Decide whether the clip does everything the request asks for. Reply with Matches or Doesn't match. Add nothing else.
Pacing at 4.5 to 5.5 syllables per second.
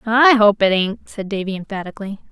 Doesn't match